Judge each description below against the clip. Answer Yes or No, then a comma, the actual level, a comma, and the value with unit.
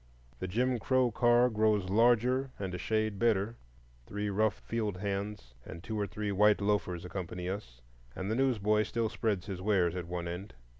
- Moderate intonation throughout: Yes, average, 3.2 semitones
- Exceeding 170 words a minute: Yes, average, 180 wpm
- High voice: No, low, 105 Hz